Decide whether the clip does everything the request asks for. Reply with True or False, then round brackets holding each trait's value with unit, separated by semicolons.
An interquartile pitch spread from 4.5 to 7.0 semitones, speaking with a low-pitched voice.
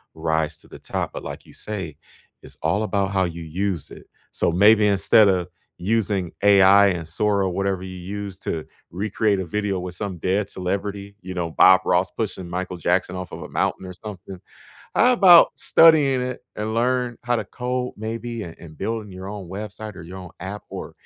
False (2.9 semitones; 100 Hz)